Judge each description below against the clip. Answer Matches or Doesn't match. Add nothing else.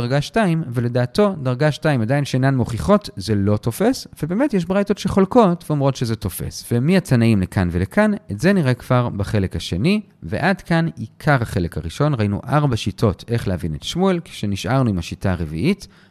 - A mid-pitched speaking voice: Doesn't match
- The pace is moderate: Doesn't match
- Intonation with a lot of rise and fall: Matches